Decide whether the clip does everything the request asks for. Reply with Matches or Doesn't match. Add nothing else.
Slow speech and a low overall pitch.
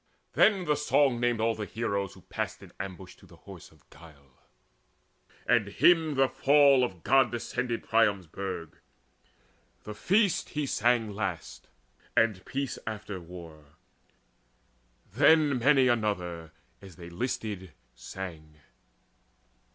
Matches